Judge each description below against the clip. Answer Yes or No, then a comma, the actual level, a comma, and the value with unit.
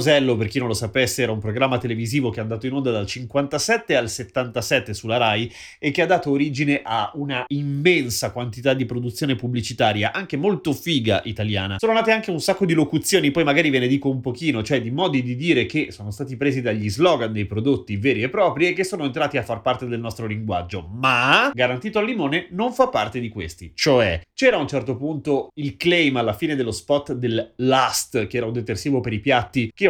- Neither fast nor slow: No, fast, 215 wpm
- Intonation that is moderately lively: Yes, average, 4.3 semitones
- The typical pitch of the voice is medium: No, low, 130 Hz